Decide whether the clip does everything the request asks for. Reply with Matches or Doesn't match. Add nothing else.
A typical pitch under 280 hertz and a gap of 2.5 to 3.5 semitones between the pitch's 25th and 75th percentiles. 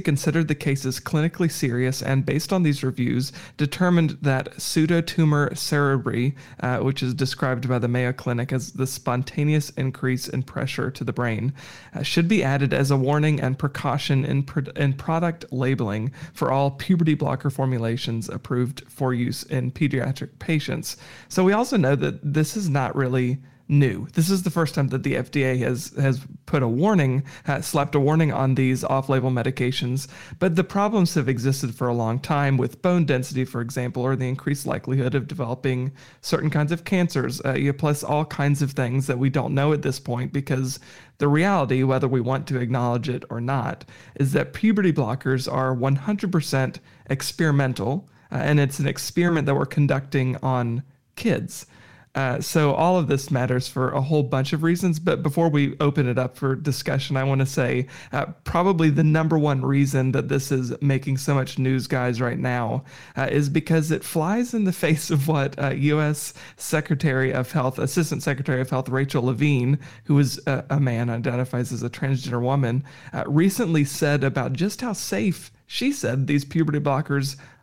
Matches